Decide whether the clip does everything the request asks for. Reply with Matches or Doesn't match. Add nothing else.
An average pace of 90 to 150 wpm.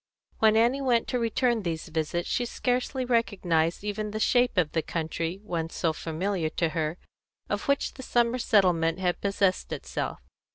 Doesn't match